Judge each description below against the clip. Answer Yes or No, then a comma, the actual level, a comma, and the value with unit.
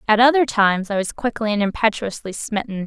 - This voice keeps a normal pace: Yes, average, 190 wpm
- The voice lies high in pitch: Yes, high, 215 Hz